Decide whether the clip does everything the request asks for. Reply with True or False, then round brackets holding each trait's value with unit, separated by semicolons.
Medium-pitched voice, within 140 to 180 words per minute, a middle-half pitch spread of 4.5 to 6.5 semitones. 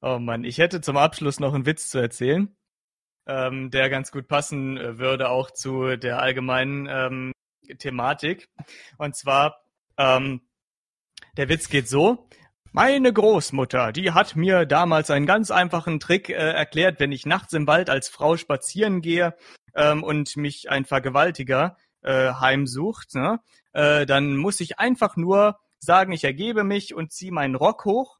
True (150 Hz; 155 wpm; 4.8 semitones)